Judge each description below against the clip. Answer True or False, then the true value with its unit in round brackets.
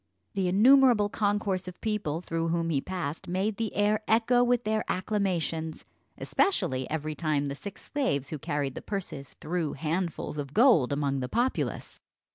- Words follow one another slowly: False (160 wpm)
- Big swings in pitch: True (5.9 semitones)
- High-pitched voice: False (180 Hz)